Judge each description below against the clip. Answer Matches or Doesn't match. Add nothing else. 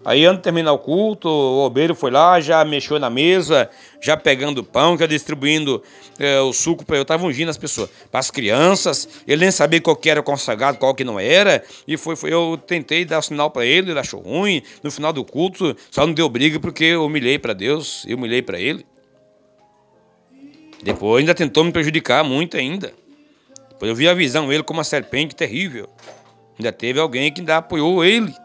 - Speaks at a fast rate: Matches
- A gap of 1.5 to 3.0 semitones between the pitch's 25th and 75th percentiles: Matches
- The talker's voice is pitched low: Doesn't match